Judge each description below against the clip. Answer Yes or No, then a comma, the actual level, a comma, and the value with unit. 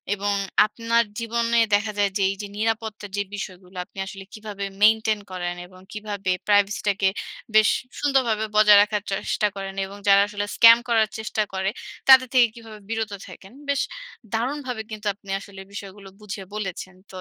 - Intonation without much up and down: Yes, narrow, 2.2 semitones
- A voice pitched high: Yes, high, 210 Hz